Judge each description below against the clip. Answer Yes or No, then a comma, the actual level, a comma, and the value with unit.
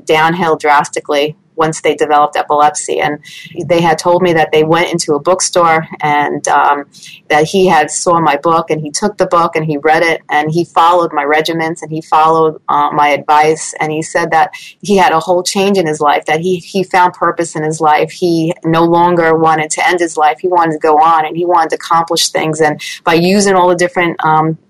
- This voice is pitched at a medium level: Yes, medium, 160 Hz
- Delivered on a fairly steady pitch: Yes, narrow, 2.1 semitones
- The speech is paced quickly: Yes, fast, 220 wpm